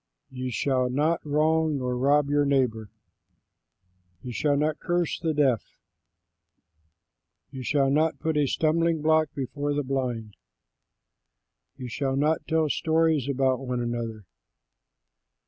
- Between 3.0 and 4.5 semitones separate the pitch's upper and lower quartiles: Yes, average, 3.5 semitones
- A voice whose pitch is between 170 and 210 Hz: No, medium, 140 Hz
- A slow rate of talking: Yes, slow, 125 wpm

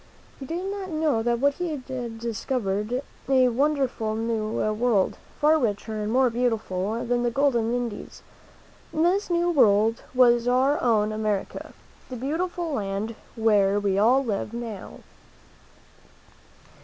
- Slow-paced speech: Yes, slow, 130 wpm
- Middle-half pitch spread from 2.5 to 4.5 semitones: Yes, average, 4.1 semitones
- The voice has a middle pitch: No, high, 240 Hz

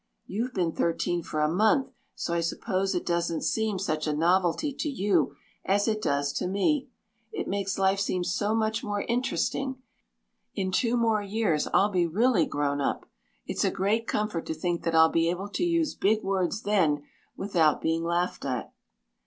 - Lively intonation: No, average, 4.5 semitones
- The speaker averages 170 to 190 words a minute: Yes, average, 180 wpm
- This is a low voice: No, high, 190 Hz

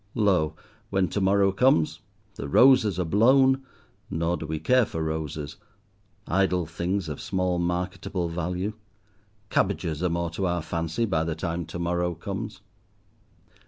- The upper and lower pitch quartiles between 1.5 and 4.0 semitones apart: Yes, average, 3.3 semitones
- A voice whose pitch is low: Yes, very low, 90 Hz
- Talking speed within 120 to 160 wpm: Yes, average, 145 wpm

